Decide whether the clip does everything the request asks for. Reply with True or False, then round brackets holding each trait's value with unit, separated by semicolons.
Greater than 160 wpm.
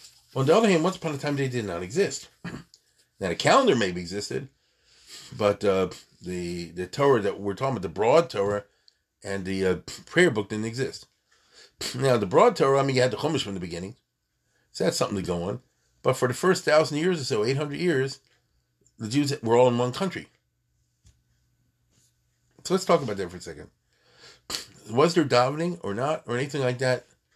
True (195 wpm)